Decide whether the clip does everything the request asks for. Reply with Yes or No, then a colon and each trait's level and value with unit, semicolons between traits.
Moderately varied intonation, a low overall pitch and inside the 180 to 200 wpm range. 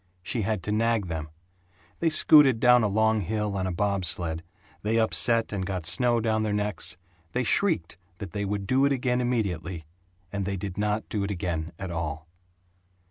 Yes: average, 3.7 semitones; low, 105 Hz; average, 190 wpm